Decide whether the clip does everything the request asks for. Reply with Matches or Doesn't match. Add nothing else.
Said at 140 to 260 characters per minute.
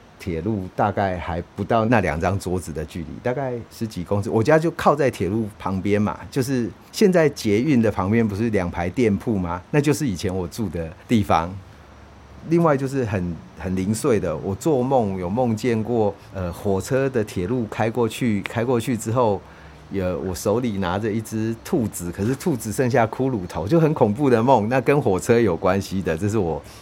Doesn't match